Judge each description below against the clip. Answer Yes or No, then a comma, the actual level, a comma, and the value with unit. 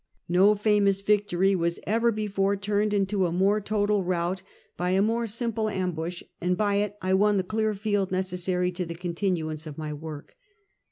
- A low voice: No, high, 195 Hz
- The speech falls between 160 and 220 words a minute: Yes, average, 175 wpm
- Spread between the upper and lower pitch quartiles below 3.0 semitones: Yes, narrow, 2.6 semitones